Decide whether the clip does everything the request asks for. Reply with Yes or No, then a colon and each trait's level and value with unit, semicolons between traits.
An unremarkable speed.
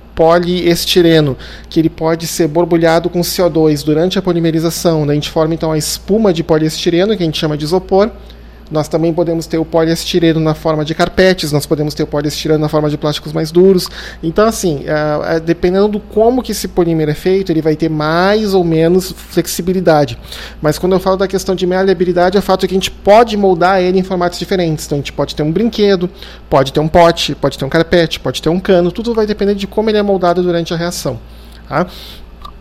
No: fast, 210 wpm